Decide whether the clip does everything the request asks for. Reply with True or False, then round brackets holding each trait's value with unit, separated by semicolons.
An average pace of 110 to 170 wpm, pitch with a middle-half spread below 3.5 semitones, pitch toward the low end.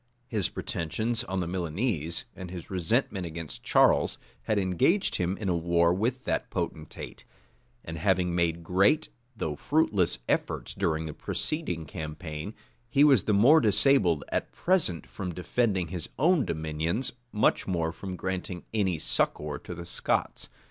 False (150 wpm; 4.7 semitones; 90 Hz)